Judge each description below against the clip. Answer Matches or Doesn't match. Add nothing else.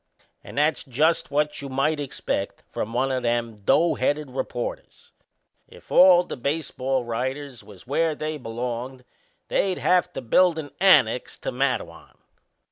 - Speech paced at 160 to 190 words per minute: Doesn't match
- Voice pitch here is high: Doesn't match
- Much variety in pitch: Doesn't match